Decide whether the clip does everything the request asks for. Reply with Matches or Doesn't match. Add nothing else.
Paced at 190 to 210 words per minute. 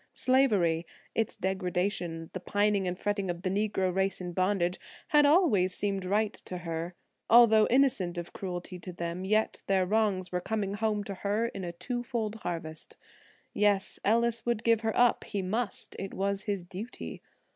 Doesn't match